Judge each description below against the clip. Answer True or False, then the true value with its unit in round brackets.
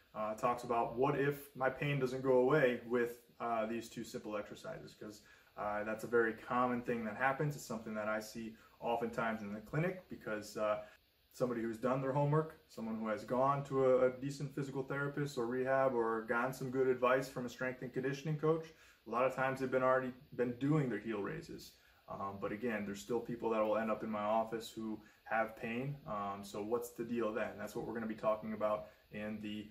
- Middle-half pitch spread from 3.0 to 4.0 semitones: True (3.3 semitones)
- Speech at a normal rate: False (220 wpm)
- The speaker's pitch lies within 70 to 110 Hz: False (120 Hz)